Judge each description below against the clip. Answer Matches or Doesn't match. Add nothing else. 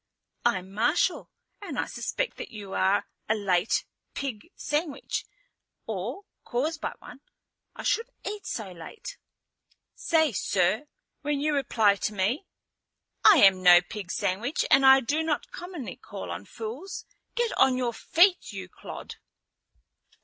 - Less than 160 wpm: Matches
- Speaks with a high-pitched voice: Matches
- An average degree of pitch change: Doesn't match